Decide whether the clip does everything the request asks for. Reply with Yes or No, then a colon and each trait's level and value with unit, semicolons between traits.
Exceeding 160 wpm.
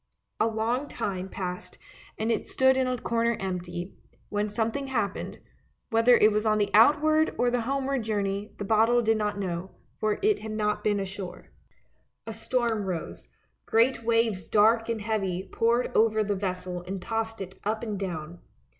Yes: average, 170 wpm